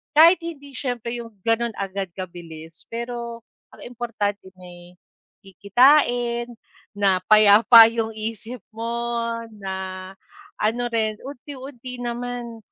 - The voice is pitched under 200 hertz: No, high, 230 Hz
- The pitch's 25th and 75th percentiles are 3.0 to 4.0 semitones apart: Yes, average, 3.4 semitones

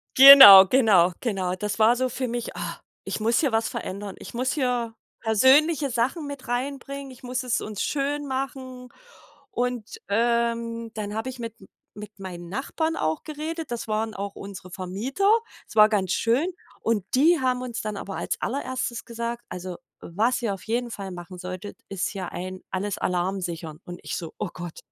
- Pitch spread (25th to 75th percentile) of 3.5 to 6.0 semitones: Yes, average, 4.8 semitones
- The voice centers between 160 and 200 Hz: No, high, 230 Hz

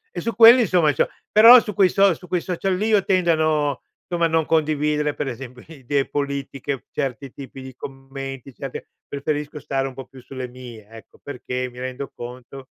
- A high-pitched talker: No, medium, 140 Hz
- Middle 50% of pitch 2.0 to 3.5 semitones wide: No, average, 4.1 semitones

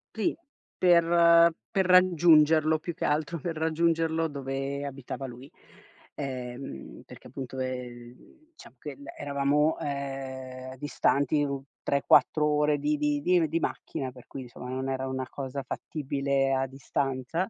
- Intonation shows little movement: No, average, 3.2 semitones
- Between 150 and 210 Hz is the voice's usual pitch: No, medium, 140 Hz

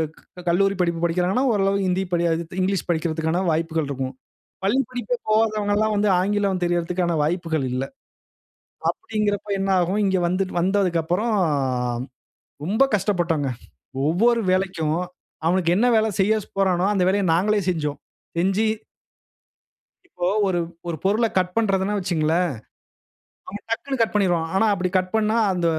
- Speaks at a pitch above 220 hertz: No, medium, 185 Hz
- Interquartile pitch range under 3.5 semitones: Yes, average, 3.1 semitones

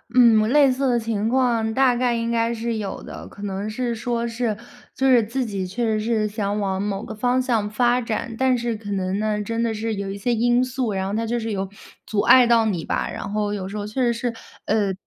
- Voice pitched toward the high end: Yes, high, 225 Hz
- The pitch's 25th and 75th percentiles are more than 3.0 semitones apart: No, narrow, 2.5 semitones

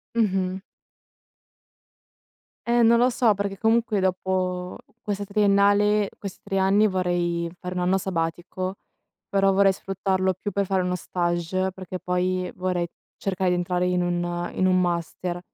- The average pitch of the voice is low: No, medium, 185 Hz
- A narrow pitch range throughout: Yes, narrow, 1.8 semitones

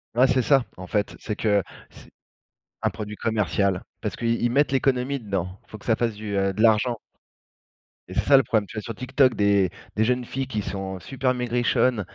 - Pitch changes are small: No, average, 3.7 semitones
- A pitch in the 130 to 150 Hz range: No, low, 115 Hz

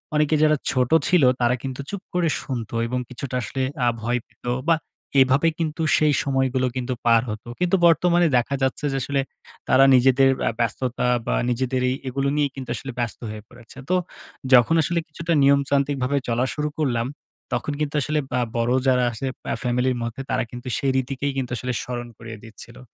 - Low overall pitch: Yes, low, 130 Hz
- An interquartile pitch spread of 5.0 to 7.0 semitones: No, average, 2.7 semitones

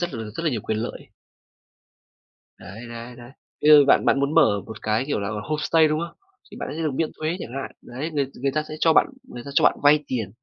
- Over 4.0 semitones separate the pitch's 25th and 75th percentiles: Yes, average, 4.7 semitones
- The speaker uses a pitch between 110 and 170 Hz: Yes, medium, 140 Hz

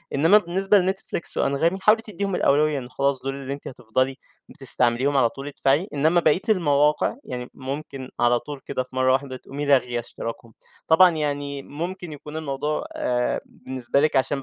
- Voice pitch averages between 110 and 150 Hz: Yes, medium, 140 Hz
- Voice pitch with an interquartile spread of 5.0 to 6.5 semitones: No, average, 3.5 semitones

